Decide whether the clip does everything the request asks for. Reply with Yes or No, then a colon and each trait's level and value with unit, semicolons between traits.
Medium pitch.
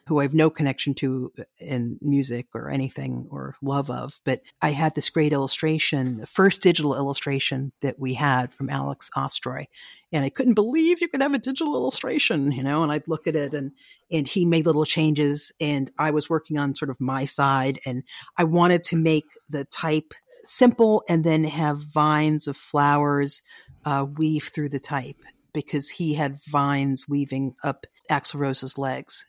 Yes: medium, 145 Hz